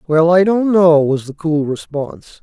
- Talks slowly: No, average, 200 wpm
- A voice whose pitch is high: No, medium, 160 Hz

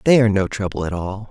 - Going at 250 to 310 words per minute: Yes, fast, 275 wpm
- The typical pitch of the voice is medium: No, low, 100 Hz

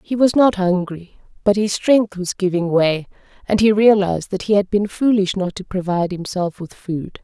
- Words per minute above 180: Yes, average, 200 wpm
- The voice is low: No, high, 195 Hz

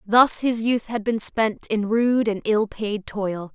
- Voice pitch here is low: No, high, 215 Hz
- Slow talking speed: No, fast, 205 wpm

